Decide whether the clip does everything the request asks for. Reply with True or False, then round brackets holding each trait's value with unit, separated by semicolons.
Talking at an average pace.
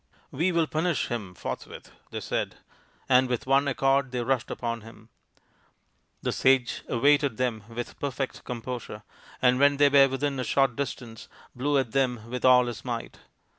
True (170 wpm)